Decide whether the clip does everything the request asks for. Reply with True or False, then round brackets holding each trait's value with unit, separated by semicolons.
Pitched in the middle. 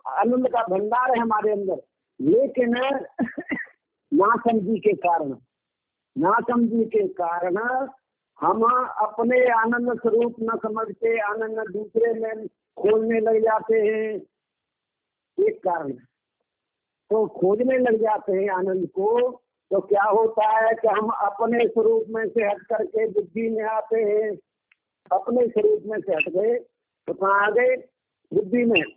False (225 Hz)